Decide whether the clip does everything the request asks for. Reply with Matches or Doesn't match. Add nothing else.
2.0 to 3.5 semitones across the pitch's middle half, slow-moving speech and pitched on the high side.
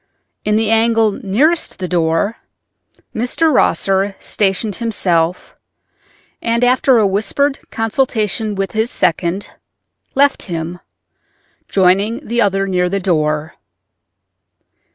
Doesn't match